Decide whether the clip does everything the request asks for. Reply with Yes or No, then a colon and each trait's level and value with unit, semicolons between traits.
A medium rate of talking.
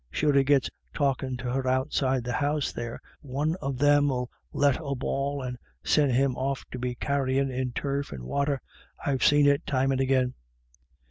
Yes: average, 190 wpm